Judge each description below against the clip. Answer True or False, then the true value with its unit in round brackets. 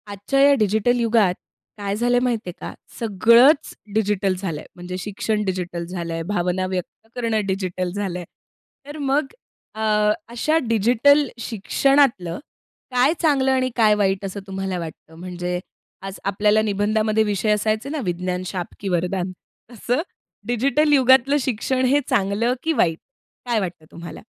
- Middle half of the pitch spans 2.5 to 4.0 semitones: False (4.9 semitones)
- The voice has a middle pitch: False (210 Hz)